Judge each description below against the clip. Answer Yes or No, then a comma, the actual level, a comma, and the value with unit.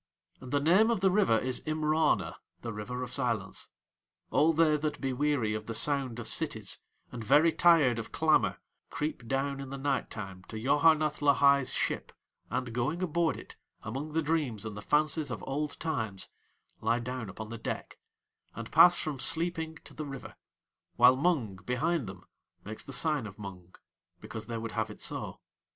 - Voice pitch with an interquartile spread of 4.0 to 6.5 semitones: Yes, average, 5.3 semitones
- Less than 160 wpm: No, average, 180 wpm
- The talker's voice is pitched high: No, low, 135 Hz